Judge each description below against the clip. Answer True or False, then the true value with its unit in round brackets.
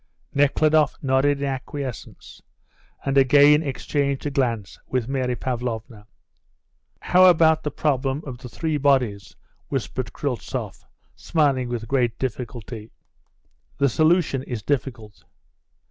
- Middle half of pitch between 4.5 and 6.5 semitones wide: False (2.9 semitones)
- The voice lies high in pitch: False (135 Hz)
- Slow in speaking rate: True (115 wpm)